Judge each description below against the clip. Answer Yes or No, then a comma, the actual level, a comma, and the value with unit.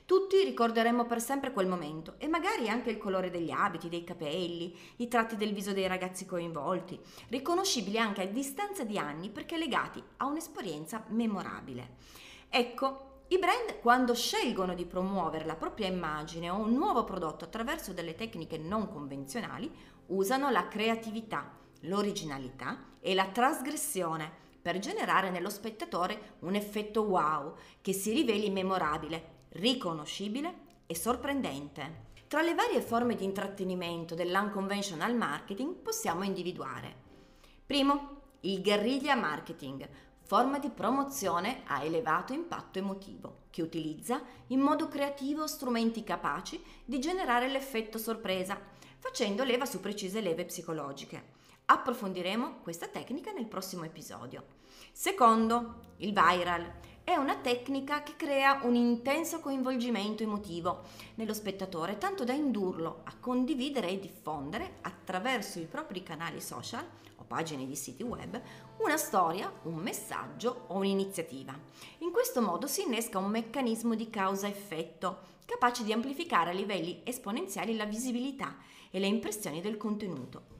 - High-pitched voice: Yes, high, 210 Hz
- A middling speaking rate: Yes, average, 130 wpm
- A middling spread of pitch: No, wide, 6.4 semitones